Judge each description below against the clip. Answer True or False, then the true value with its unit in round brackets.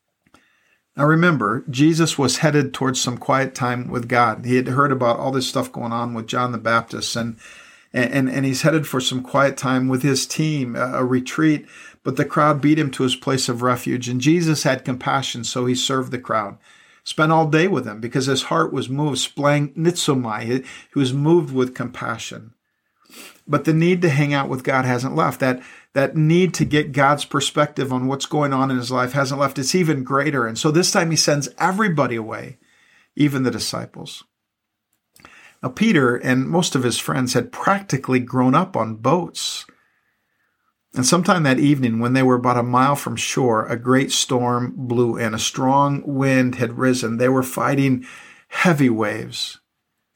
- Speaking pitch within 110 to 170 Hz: True (135 Hz)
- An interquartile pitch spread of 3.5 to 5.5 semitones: False (2.8 semitones)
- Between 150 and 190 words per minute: True (185 wpm)